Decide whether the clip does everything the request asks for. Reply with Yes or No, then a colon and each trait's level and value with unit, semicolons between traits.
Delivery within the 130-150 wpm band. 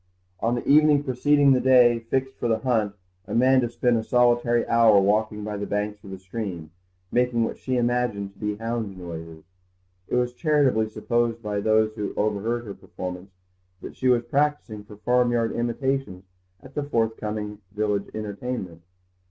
No: average, 165 wpm